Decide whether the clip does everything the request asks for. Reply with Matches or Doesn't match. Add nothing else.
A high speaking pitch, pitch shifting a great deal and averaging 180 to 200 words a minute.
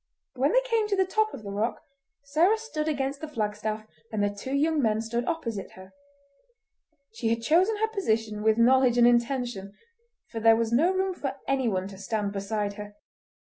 Matches